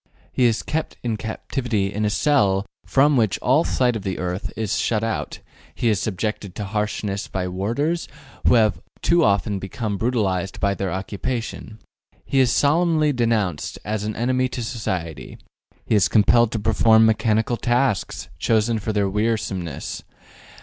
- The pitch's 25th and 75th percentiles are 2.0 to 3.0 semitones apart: No, average, 3.4 semitones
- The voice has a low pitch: Yes, low, 110 Hz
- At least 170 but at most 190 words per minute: No, average, 155 wpm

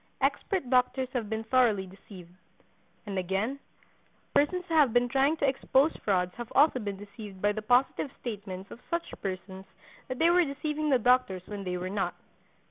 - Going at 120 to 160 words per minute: No, average, 175 wpm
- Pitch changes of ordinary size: No, wide, 5.7 semitones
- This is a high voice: Yes, high, 230 Hz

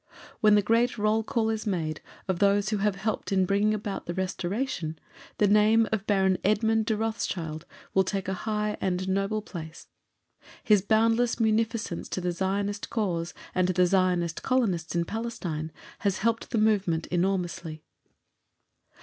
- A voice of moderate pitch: No, high, 200 Hz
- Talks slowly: No, average, 160 wpm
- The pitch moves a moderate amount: Yes, average, 3.3 semitones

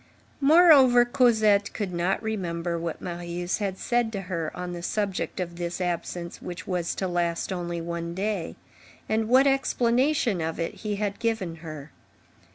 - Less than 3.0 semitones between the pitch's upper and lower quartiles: No, average, 4.4 semitones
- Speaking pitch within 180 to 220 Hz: Yes, medium, 185 Hz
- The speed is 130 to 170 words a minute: Yes, average, 160 wpm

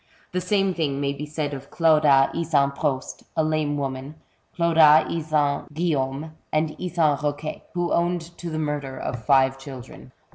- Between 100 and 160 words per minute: Yes, average, 155 wpm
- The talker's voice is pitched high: No, medium, 150 Hz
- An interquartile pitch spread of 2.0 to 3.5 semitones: Yes, average, 2.8 semitones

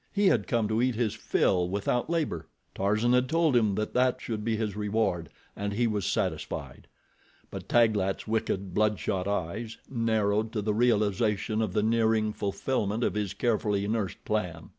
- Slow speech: No, average, 160 wpm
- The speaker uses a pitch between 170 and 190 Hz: No, low, 110 Hz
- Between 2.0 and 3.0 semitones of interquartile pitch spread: Yes, narrow, 2.4 semitones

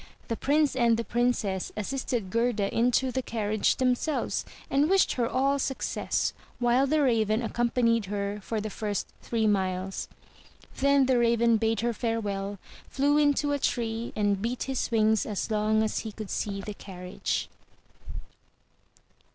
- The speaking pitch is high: Yes, high, 230 Hz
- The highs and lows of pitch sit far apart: No, average, 3.3 semitones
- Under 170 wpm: Yes, average, 150 wpm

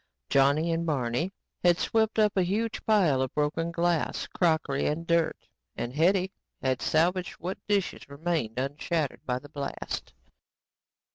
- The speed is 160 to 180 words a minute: No, average, 140 wpm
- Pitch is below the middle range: No, medium, 165 Hz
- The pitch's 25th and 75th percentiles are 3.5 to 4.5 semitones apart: Yes, average, 4.2 semitones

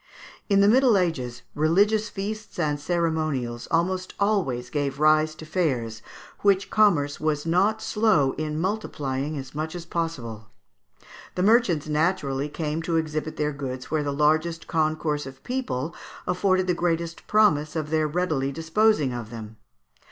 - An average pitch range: Yes, average, 4.1 semitones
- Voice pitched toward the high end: No, medium, 155 Hz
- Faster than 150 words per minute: No, average, 145 wpm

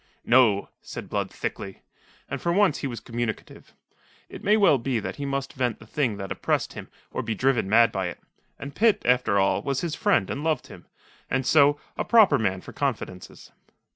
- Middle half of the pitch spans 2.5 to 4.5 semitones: No, average, 4.9 semitones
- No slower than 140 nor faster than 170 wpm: No, average, 200 wpm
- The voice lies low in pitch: Yes, low, 130 Hz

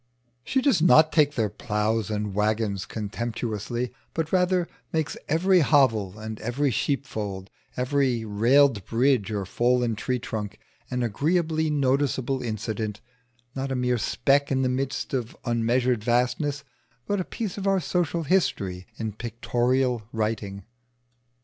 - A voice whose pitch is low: Yes, low, 125 Hz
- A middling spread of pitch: Yes, average, 4.8 semitones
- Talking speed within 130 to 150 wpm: Yes, slow, 135 wpm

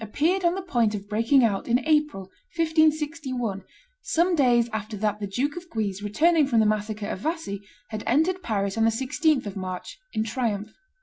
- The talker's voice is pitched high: Yes, high, 235 Hz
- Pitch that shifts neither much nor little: No, wide, 6.9 semitones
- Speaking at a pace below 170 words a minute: No, average, 185 wpm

